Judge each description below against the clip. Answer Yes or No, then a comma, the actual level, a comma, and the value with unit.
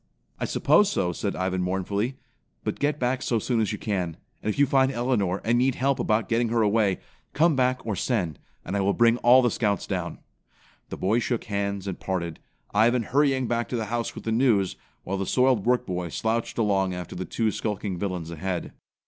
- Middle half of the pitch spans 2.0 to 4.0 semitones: No, average, 4.4 semitones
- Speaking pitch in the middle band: No, low, 110 Hz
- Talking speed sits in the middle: No, fast, 210 wpm